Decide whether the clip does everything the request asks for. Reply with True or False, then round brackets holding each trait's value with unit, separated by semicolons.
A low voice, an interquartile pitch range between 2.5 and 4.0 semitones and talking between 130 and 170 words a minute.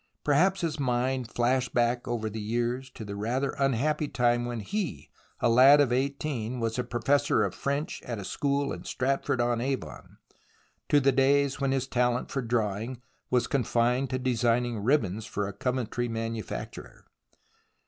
True (125 Hz; 2.8 semitones; 160 wpm)